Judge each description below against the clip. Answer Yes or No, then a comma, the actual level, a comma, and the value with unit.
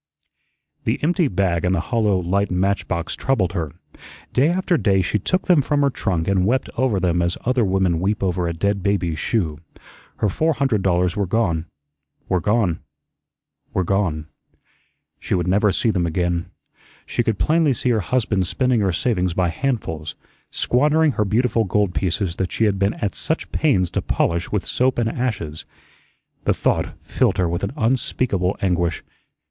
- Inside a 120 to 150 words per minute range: No, average, 175 wpm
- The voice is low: Yes, low, 100 Hz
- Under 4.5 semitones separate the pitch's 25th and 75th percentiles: No, average, 5.2 semitones